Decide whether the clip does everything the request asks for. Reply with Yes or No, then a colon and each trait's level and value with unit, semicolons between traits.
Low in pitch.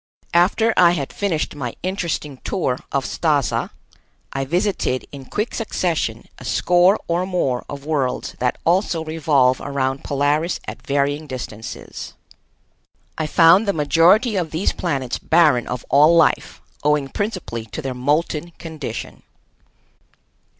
No: medium, 155 Hz